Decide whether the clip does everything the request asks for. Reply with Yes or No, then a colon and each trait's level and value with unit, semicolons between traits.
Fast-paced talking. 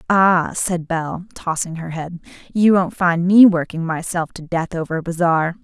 No: average, 180 wpm